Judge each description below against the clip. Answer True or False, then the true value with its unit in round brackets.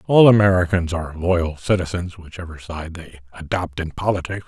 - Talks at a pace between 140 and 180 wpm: True (145 wpm)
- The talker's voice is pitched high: False (90 Hz)